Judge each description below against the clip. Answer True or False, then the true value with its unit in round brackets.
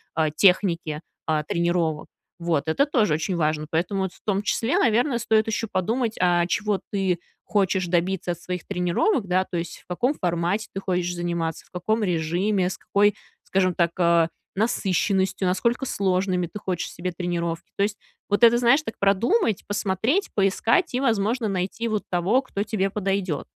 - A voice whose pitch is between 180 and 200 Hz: True (190 Hz)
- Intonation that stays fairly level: False (3.6 semitones)